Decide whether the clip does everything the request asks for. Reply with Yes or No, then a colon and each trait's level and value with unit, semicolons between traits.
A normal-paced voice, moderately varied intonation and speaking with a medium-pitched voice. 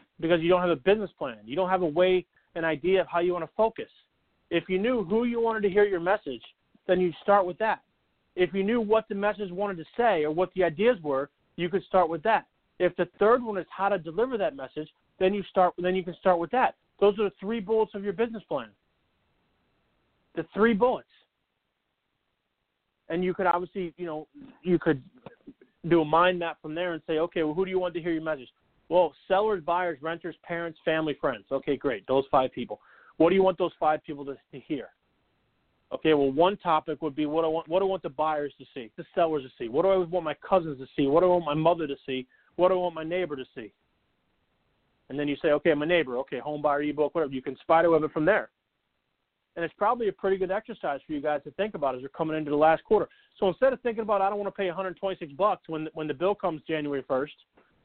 No: fast, 250 wpm; average, 3.9 semitones; medium, 175 Hz